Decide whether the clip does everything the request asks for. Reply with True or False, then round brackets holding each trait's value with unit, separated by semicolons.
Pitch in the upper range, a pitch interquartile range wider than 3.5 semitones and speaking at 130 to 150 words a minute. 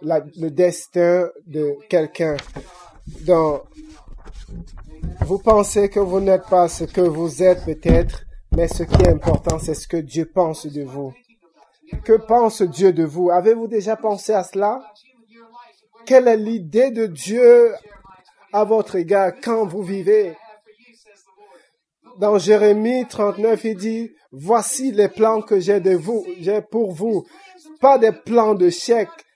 True (205 Hz; 4.3 semitones; 140 wpm)